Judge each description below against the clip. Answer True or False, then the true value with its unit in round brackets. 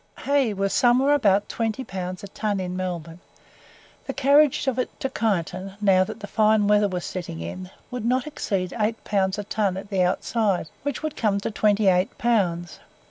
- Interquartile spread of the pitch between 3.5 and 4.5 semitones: True (3.9 semitones)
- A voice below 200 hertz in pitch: False (205 Hz)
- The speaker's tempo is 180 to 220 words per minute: True (185 wpm)